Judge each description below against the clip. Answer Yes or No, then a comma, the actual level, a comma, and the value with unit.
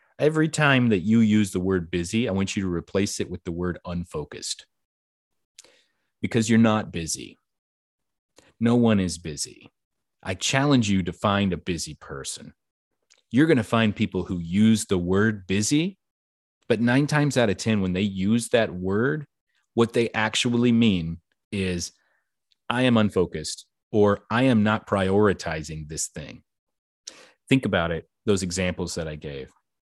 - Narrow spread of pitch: No, average, 4.4 semitones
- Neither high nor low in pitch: No, low, 100 Hz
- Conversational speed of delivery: Yes, average, 155 wpm